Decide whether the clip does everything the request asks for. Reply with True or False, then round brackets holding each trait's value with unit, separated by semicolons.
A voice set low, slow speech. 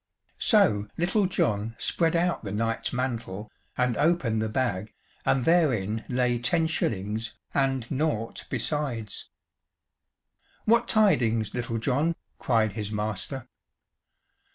True (120 Hz; 110 wpm)